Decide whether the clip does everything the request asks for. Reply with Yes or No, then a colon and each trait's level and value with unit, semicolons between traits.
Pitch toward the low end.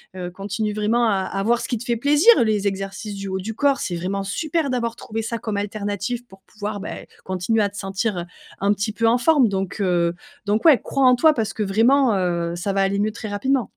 No: high, 210 Hz